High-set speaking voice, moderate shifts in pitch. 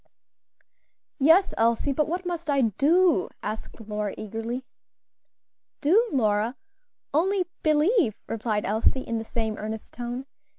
No: high, 245 Hz; wide, 6.4 semitones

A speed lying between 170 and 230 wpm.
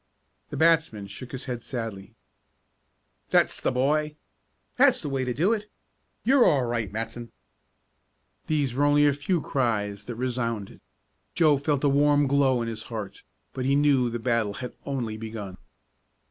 No: average, 160 wpm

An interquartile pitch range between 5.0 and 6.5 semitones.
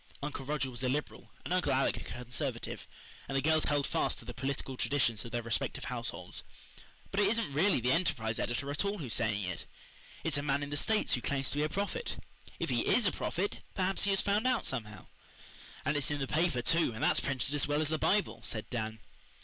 Yes: wide, 5.4 semitones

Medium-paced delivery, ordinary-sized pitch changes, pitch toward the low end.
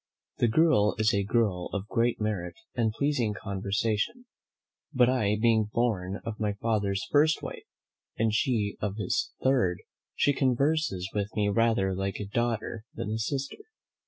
Yes: average, 155 wpm; average, 3.1 semitones; low, 110 Hz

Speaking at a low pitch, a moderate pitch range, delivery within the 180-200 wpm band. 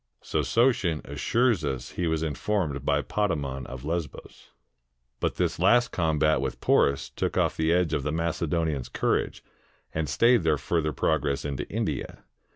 No: very low, 80 Hz; average, 3.3 semitones; average, 155 wpm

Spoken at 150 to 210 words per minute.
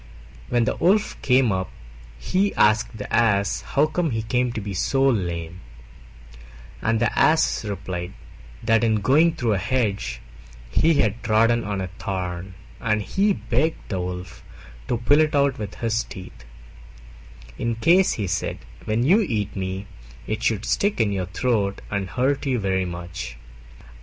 Yes: average, 155 wpm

